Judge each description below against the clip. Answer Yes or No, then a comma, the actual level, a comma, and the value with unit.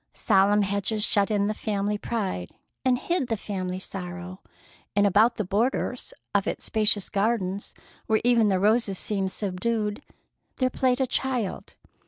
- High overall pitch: Yes, high, 210 Hz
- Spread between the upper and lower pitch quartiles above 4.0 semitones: No, average, 3.1 semitones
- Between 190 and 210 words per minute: No, average, 150 wpm